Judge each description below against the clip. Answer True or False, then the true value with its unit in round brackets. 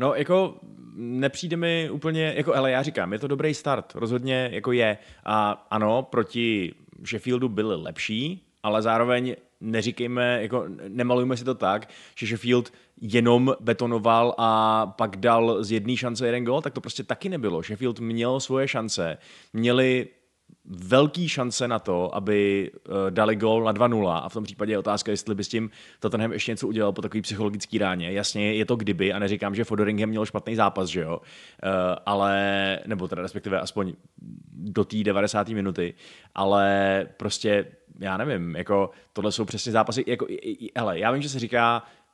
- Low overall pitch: True (110 Hz)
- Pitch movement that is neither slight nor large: True (3.1 semitones)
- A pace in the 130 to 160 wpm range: False (170 wpm)